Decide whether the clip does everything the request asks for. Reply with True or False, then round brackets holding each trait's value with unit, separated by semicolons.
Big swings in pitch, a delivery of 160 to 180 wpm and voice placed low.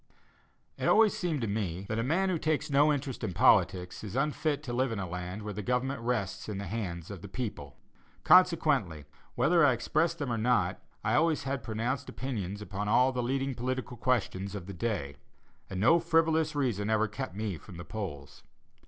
False (5.7 semitones; 195 wpm; 115 Hz)